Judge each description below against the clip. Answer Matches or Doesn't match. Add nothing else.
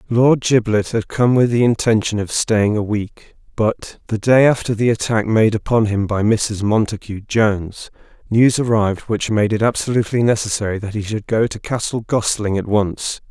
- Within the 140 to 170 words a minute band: Doesn't match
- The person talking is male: Matches